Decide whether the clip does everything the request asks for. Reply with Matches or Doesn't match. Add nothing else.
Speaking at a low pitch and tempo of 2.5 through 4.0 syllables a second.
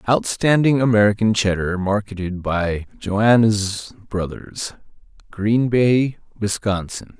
Matches